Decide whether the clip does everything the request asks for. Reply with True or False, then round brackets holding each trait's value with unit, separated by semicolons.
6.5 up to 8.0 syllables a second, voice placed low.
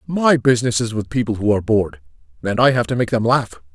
True (6.6 syllables/s; 110 Hz)